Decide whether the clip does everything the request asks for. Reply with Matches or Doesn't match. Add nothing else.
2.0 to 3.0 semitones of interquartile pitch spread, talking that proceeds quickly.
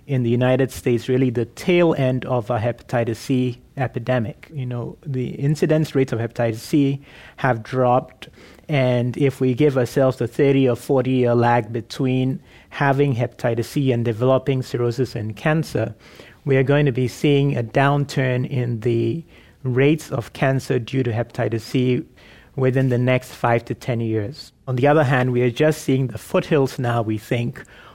Doesn't match